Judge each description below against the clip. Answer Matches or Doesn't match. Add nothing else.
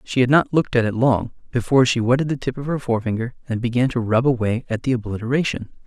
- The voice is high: Doesn't match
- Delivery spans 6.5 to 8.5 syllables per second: Matches